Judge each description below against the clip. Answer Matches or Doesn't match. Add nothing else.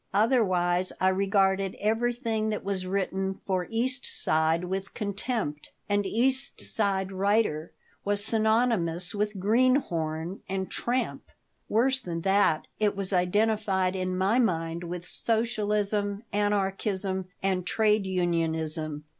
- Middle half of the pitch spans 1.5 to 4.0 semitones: Matches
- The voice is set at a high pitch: Matches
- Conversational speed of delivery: Doesn't match